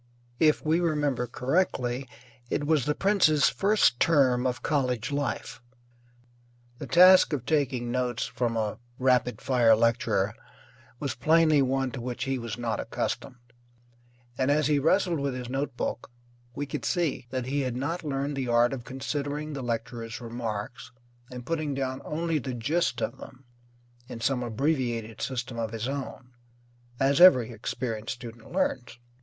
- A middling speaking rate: Yes, average, 150 wpm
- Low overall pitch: Yes, low, 130 Hz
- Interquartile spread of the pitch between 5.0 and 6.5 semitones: No, average, 3.3 semitones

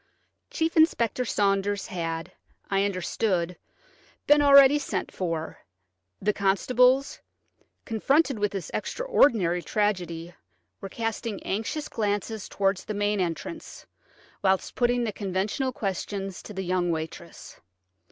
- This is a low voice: No, high, 205 Hz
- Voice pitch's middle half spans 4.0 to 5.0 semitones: Yes, average, 4.4 semitones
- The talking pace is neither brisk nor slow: No, slow, 115 wpm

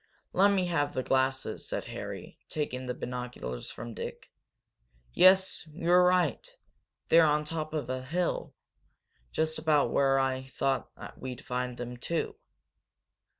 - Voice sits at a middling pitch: Yes, medium, 145 Hz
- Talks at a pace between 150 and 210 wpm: No, average, 140 wpm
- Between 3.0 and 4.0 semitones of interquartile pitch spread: No, average, 4.6 semitones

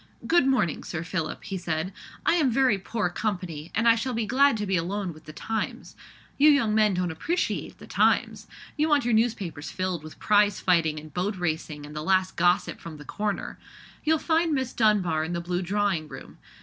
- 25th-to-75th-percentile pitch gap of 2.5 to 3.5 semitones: No, wide, 5.4 semitones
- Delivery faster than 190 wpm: Yes, average, 200 wpm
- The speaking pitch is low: No, high, 190 Hz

